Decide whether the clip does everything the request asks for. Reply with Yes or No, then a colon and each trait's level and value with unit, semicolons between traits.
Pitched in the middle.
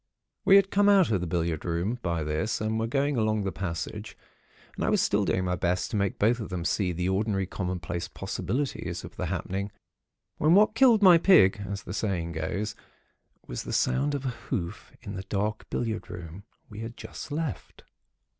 No: low, 105 Hz